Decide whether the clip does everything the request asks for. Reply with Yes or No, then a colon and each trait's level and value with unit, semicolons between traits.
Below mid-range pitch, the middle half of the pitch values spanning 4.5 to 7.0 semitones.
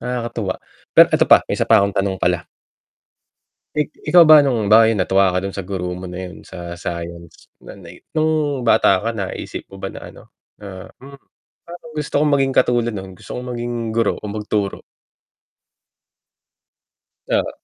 Yes: low, 105 Hz; average, 5.0 semitones